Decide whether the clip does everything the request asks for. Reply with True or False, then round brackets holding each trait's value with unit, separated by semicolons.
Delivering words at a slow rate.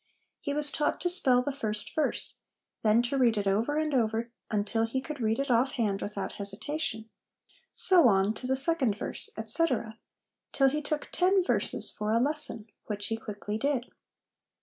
False (175 wpm)